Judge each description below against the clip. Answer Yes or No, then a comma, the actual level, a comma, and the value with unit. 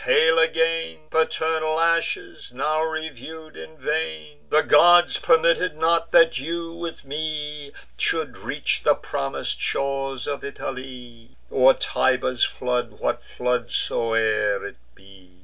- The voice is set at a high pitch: No, medium, 145 Hz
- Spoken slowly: Yes, slow, 120 wpm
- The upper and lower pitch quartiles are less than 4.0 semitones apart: No, average, 4.8 semitones